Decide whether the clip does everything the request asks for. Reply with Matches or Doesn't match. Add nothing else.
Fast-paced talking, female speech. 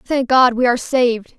Matches